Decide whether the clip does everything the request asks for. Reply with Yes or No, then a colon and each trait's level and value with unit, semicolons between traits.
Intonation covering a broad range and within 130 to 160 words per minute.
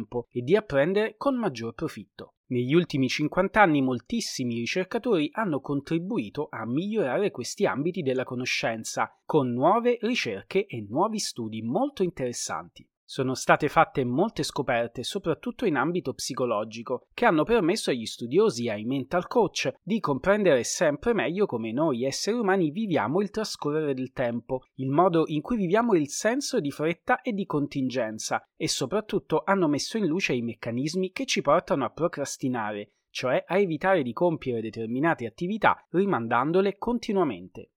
Yes: wide, 7.9 semitones; average, 150 wpm